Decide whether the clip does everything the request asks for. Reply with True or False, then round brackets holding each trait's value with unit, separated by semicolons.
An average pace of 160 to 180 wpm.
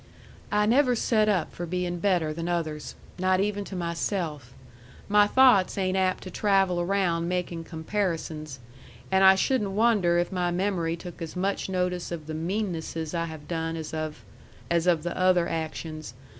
True (170 wpm)